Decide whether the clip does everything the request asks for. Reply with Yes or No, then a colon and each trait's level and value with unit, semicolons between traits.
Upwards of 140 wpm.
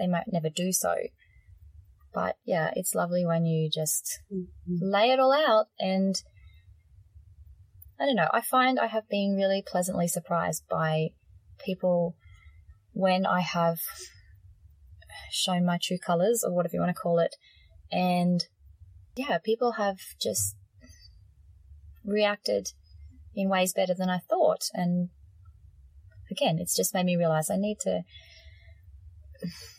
No: slow, 135 wpm